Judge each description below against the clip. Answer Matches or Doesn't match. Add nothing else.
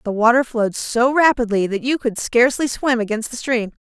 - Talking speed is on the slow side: Doesn't match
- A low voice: Doesn't match